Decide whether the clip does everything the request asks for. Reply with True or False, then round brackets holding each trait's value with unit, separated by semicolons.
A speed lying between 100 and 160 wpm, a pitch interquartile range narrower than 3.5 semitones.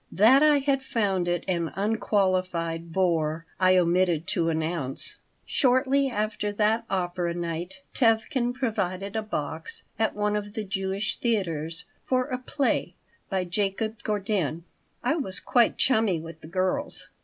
False (140 wpm; 4.6 semitones)